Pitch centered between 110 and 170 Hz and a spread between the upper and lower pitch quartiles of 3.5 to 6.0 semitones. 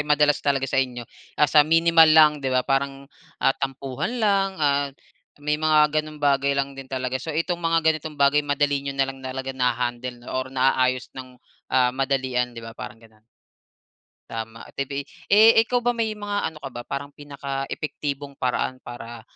No: medium, 140 Hz; average, 2.8 semitones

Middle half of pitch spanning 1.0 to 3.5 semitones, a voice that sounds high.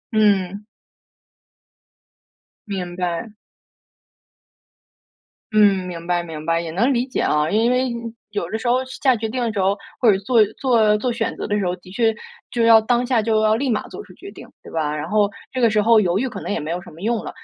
No: average, 4.6 semitones; high, 210 Hz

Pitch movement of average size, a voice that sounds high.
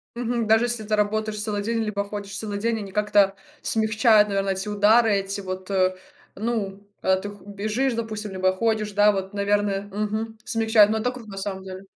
No: narrow, 1.9 semitones; high, 210 Hz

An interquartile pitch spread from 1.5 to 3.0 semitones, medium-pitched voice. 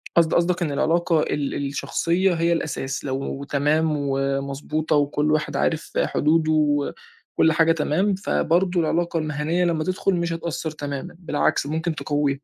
Yes: narrow, 2.6 semitones; medium, 155 Hz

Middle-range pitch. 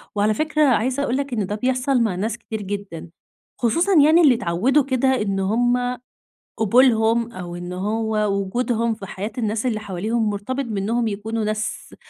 No: high, 225 Hz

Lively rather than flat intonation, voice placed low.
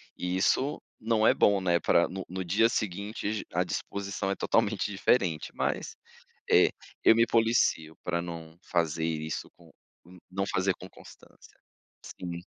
No: average, 3.2 semitones; very low, 95 Hz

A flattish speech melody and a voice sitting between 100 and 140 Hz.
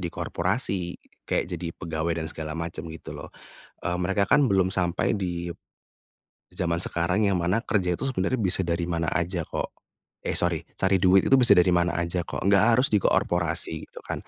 No: narrow, 2.1 semitones; very low, 90 Hz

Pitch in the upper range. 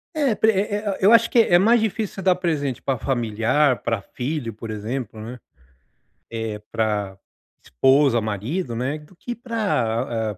No: low, 135 Hz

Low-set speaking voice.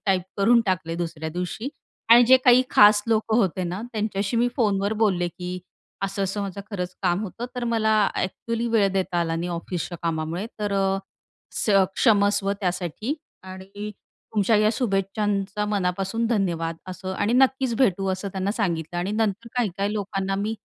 No: high, 195 Hz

